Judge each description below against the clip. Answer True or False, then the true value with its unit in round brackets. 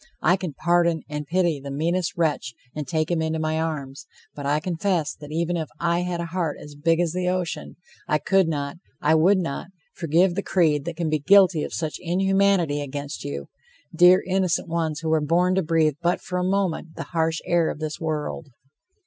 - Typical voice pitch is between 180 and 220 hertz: False (165 Hz)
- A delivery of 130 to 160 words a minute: False (205 wpm)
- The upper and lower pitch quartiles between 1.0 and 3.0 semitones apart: True (2.7 semitones)